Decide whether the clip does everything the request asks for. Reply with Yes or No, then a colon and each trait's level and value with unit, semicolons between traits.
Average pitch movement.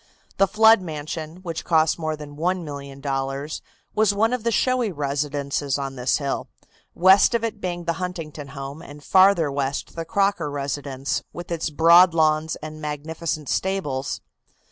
Yes: average, 4.3 semitones